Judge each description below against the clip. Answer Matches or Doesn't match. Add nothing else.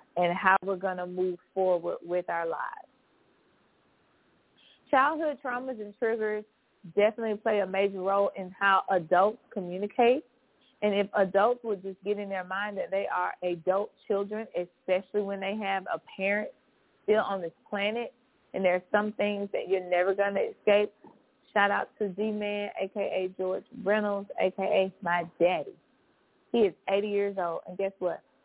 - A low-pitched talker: Doesn't match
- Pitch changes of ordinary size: Doesn't match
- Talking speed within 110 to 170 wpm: Matches